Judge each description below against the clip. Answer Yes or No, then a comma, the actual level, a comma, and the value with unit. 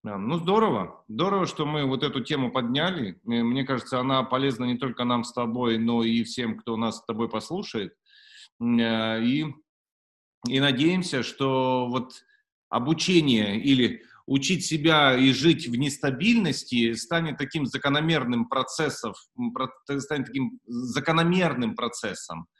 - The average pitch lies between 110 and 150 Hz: Yes, low, 135 Hz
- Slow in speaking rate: No, average, 125 wpm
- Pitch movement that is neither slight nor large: Yes, average, 4.7 semitones